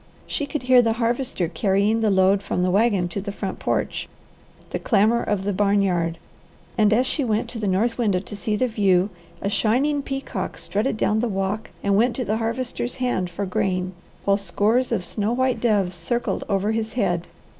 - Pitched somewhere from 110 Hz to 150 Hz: No, high, 210 Hz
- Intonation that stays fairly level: No, average, 3.4 semitones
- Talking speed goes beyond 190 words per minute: Yes, average, 200 wpm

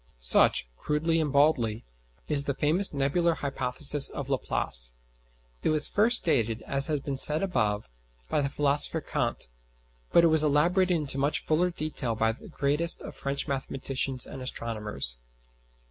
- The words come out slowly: No, average, 150 wpm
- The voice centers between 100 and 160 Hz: Yes, medium, 140 Hz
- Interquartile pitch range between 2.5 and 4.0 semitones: Yes, average, 3.6 semitones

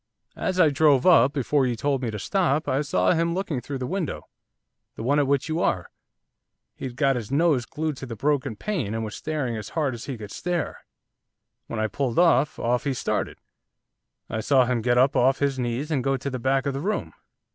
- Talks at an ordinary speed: No, fast, 220 wpm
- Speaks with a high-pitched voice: No, low, 135 Hz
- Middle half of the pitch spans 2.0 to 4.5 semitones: Yes, average, 3.7 semitones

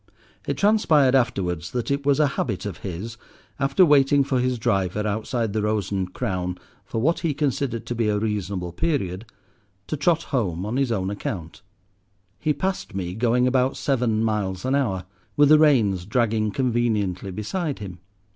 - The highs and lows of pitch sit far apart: Yes, wide, 5.8 semitones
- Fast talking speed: No, average, 170 wpm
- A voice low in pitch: Yes, low, 115 Hz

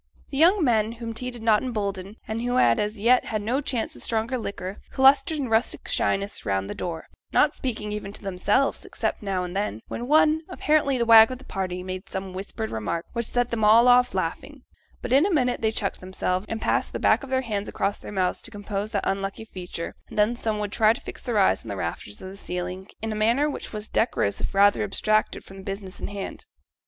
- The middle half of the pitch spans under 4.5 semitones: Yes, average, 4.1 semitones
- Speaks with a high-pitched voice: Yes, high, 215 Hz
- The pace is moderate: No, fast, 230 wpm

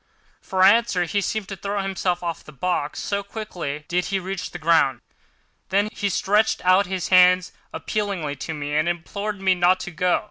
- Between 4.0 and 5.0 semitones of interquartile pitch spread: No, narrow, 2.6 semitones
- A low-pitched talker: No, medium, 185 Hz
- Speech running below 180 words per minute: No, average, 185 wpm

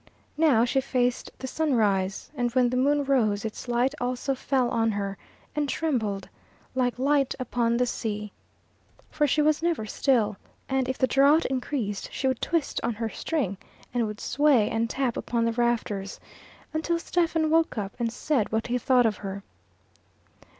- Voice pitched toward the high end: Yes, high, 245 Hz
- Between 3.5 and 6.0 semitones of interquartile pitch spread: Yes, average, 4.0 semitones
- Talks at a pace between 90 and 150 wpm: No, average, 170 wpm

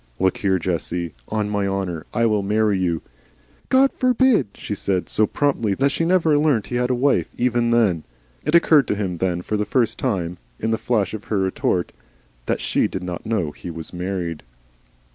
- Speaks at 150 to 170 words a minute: No, average, 200 wpm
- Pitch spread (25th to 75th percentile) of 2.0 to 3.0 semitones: No, average, 5.3 semitones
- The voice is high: No, low, 105 Hz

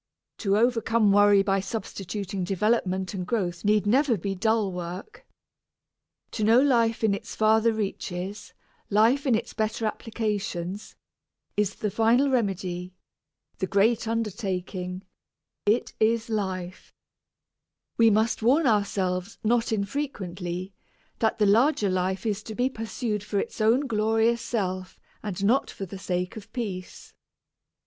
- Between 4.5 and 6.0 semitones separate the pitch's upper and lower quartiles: No, average, 3.1 semitones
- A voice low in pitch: No, high, 210 Hz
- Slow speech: Yes, slow, 130 wpm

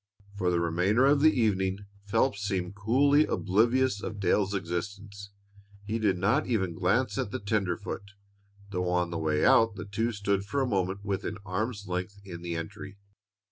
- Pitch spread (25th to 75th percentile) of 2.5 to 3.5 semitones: Yes, average, 2.9 semitones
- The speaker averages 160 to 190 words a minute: Yes, average, 170 wpm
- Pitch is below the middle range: Yes, low, 100 Hz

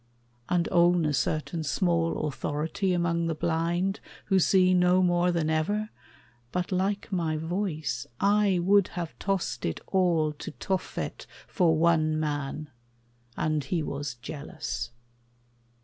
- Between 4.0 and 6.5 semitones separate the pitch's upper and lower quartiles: No, average, 2.9 semitones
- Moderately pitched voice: Yes, medium, 170 Hz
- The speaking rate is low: Yes, slow, 130 wpm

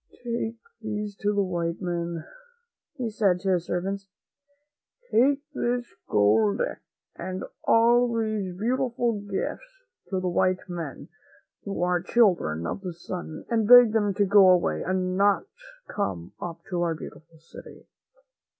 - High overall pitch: Yes, high, 195 Hz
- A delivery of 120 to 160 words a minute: Yes, average, 145 wpm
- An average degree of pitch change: Yes, average, 4.4 semitones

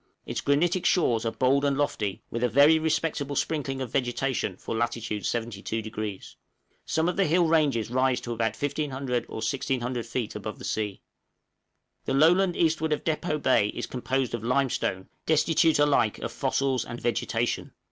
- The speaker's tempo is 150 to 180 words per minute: Yes, average, 165 wpm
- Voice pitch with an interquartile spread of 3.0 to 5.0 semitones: Yes, average, 4.6 semitones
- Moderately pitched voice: No, low, 130 Hz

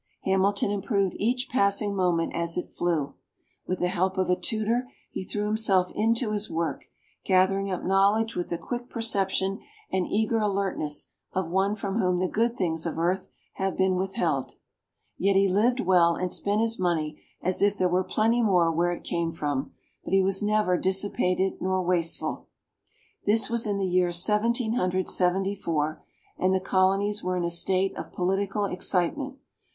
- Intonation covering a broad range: No, narrow, 2.5 semitones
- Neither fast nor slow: Yes, average, 175 wpm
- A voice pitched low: No, high, 190 Hz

